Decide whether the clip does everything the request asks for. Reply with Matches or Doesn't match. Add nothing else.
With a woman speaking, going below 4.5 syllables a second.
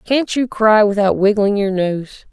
Matches